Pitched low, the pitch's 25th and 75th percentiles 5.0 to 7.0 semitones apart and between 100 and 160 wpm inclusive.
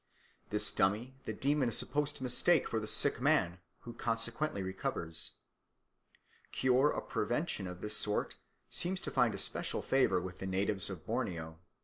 Yes: low, 115 Hz; wide, 5.6 semitones; average, 155 wpm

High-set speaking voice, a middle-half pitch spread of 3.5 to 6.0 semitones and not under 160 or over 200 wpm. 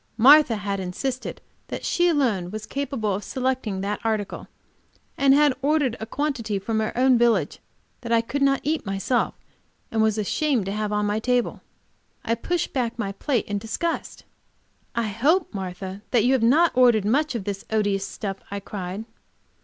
Yes: high, 225 Hz; average, 4.6 semitones; average, 175 wpm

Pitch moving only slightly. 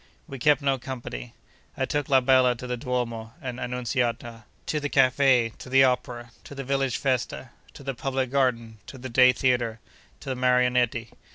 Yes: narrow, 1.9 semitones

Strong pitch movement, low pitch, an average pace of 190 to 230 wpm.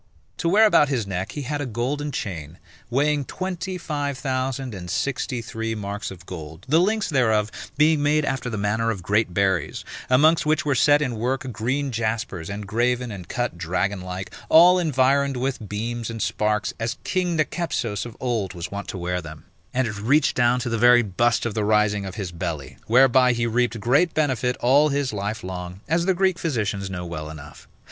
Yes: wide, 5.8 semitones; low, 120 Hz; average, 195 wpm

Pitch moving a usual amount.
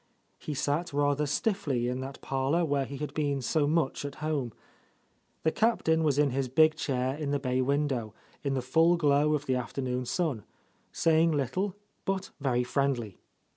Yes: average, 3.1 semitones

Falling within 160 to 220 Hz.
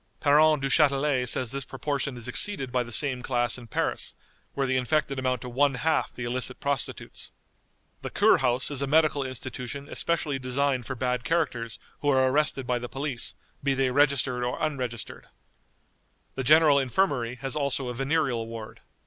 No: low, 135 Hz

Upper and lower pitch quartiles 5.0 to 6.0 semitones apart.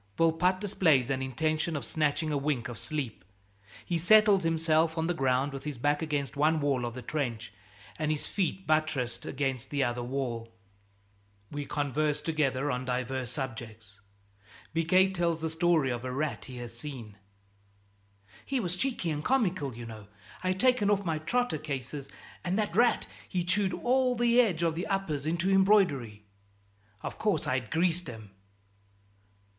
Yes: wide, 5.4 semitones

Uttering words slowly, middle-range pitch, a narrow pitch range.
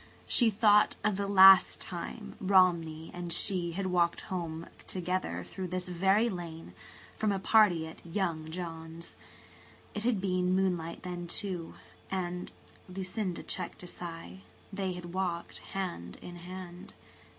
Yes: slow, 130 wpm; medium, 180 Hz; narrow, 2.1 semitones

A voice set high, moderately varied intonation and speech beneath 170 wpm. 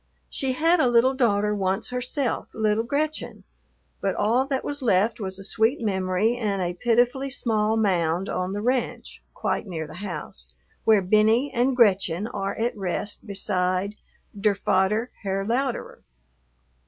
Yes: high, 215 Hz; average, 4.2 semitones; average, 150 wpm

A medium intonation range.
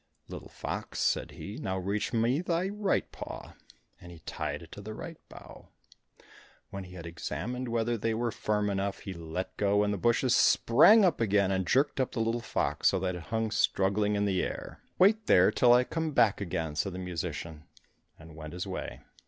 Yes: average, 4.6 semitones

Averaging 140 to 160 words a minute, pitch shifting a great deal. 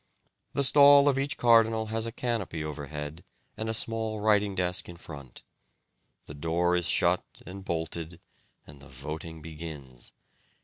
Yes: average, 145 wpm; wide, 6.3 semitones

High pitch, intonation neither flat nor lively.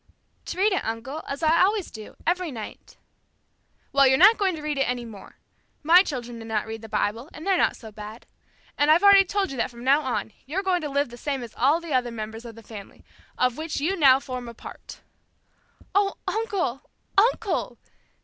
No: very high, 275 Hz; wide, 7.2 semitones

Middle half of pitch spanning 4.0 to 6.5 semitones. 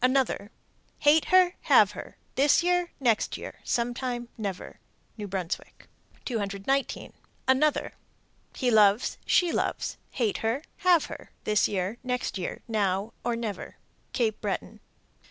Yes: average, 4.9 semitones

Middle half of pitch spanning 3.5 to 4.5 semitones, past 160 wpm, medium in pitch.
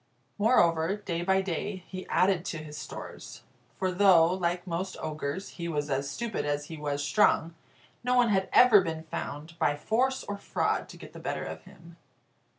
Yes: average, 3.9 semitones; average, 180 wpm; medium, 175 Hz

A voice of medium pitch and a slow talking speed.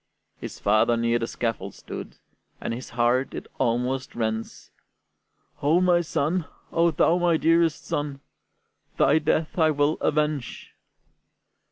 Yes: medium, 145 Hz; slow, 125 wpm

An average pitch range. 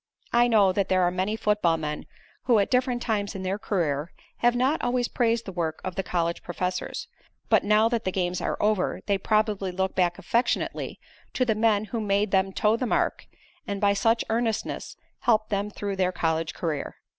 Yes: average, 3.5 semitones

